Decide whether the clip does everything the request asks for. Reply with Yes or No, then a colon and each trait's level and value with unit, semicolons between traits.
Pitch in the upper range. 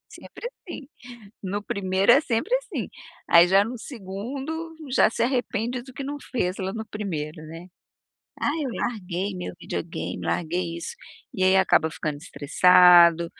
Yes: high, 195 Hz